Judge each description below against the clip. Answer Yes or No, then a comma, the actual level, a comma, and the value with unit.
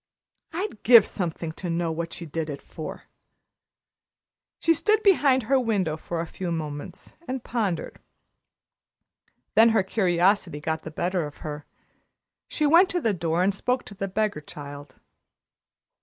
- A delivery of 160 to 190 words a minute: No, average, 150 wpm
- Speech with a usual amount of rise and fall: No, wide, 6.2 semitones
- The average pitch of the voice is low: No, medium, 185 Hz